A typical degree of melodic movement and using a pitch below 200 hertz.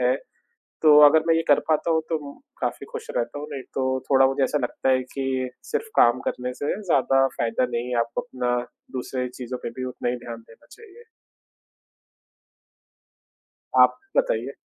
Yes: average, 4.0 semitones; low, 135 Hz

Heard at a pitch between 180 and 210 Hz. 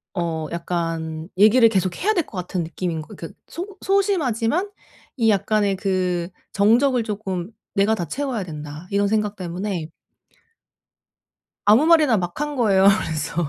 Yes: high, 200 Hz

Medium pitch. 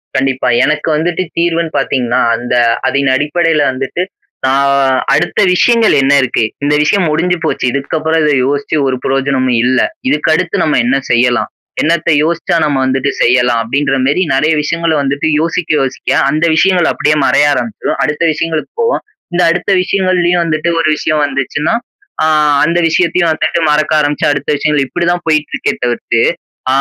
Yes: medium, 150 Hz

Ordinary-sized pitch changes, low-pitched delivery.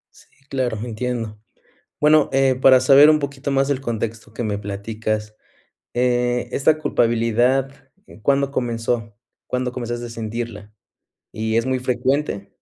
Yes: average, 3.1 semitones; low, 120 Hz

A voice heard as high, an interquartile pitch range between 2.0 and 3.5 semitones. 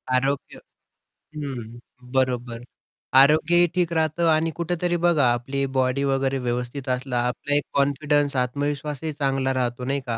No: medium, 140 Hz; average, 2.9 semitones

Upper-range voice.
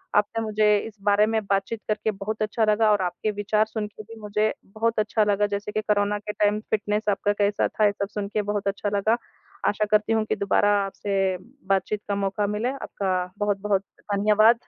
Yes: high, 210 Hz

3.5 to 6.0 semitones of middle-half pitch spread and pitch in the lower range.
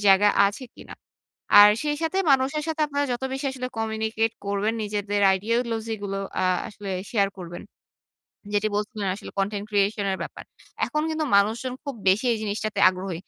No: average, 3.9 semitones; high, 215 Hz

